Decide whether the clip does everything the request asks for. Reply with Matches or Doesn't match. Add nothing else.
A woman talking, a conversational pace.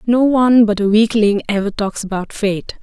Matches